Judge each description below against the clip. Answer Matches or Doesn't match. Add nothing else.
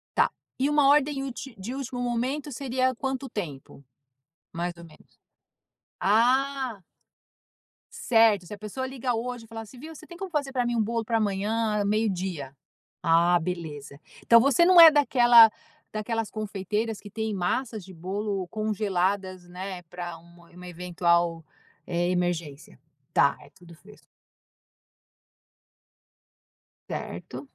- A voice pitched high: Matches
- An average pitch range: Doesn't match